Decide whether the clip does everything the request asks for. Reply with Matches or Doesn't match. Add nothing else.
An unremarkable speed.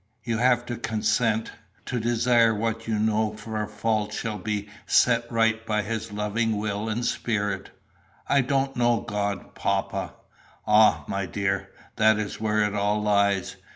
Matches